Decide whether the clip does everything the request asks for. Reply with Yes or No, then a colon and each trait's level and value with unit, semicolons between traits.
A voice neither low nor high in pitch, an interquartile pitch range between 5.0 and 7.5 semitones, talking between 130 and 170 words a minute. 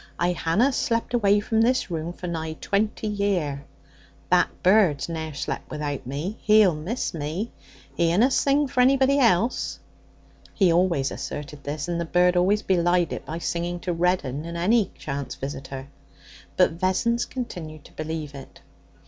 Yes: medium, 175 Hz; average, 5.3 semitones; average, 155 wpm